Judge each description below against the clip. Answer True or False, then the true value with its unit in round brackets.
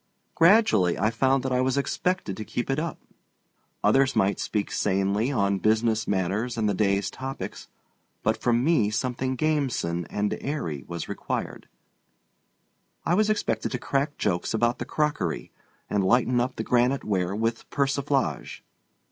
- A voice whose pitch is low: True (120 Hz)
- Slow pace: False (150 wpm)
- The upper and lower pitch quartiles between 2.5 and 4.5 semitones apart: False (5.2 semitones)